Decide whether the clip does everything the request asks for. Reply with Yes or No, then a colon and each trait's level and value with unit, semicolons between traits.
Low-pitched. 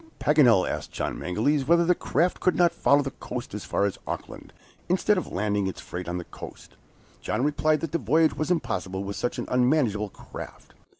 Yes: low, 130 Hz